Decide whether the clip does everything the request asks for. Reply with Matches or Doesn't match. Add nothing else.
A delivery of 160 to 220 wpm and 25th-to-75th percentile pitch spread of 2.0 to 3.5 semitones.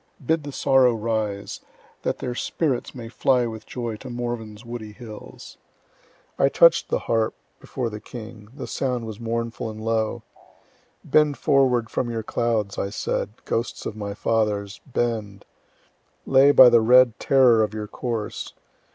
Doesn't match